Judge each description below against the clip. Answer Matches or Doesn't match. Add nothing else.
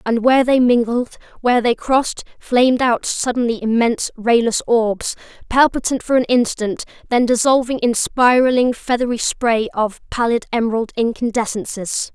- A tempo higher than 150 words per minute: Doesn't match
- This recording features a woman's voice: Matches